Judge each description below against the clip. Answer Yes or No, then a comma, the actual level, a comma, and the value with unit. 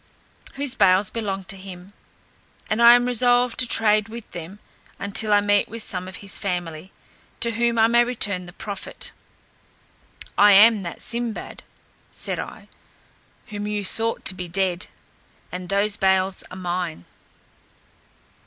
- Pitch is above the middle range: Yes, high, 205 Hz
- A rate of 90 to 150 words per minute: Yes, average, 145 wpm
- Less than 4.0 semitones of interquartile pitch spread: Yes, average, 3.6 semitones